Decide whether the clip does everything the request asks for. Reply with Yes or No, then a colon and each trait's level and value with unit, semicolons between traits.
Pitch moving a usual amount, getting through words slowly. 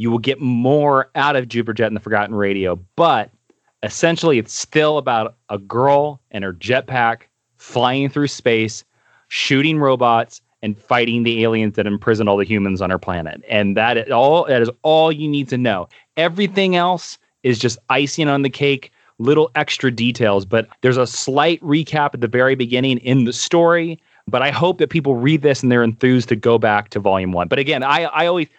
No: average, 4.2 semitones; average, 195 wpm